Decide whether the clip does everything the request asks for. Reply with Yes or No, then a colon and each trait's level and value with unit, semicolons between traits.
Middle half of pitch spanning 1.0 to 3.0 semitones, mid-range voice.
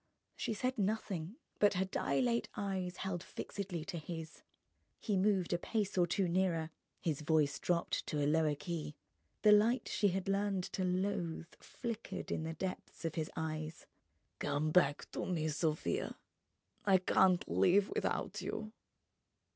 No: average, 3.8 semitones; medium, 180 Hz